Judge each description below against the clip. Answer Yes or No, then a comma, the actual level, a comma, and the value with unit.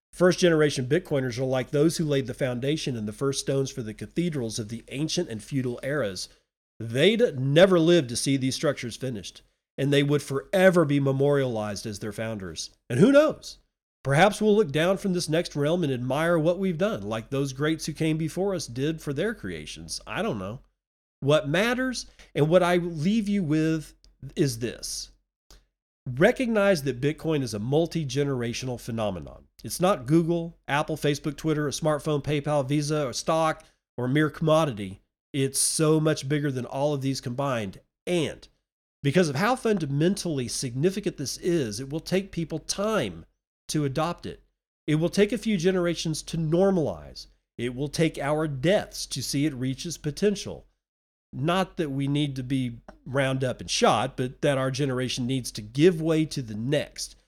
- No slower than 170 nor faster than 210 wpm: Yes, average, 175 wpm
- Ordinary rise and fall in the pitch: Yes, average, 4.5 semitones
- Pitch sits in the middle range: Yes, medium, 145 Hz